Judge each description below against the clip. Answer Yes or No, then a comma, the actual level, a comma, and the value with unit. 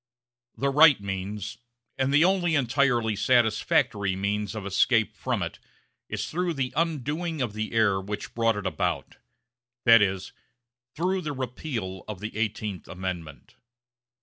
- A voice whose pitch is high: No, low, 115 Hz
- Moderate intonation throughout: No, wide, 5.7 semitones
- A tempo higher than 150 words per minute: No, average, 140 wpm